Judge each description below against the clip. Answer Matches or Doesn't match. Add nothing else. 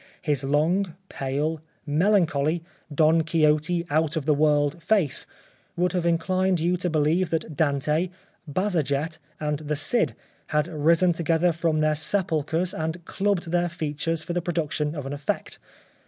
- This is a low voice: Doesn't match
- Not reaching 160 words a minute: Matches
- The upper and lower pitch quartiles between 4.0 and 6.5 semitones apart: Doesn't match